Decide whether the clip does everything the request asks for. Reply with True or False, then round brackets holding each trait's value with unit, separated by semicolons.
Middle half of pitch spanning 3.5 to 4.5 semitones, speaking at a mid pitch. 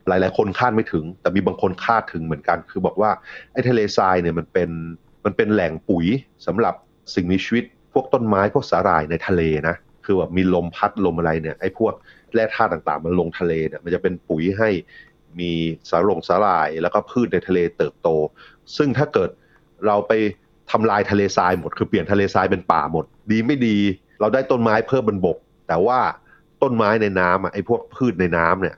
False (3.9 semitones; 95 Hz)